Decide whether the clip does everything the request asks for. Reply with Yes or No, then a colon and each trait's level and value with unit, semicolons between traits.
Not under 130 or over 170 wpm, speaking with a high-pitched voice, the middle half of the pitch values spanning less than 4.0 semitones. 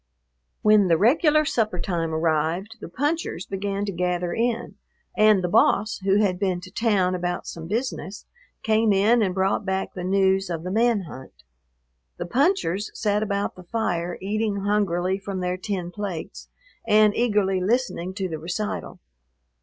Yes: average, 160 wpm; high, 195 Hz; average, 3.1 semitones